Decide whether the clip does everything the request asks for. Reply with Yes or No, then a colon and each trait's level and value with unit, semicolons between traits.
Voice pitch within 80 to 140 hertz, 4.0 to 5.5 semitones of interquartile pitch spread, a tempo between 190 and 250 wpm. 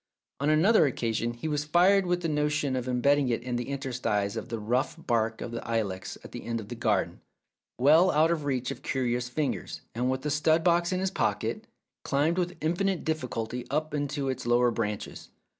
Yes: low, 135 Hz; average, 4.7 semitones; fast, 205 wpm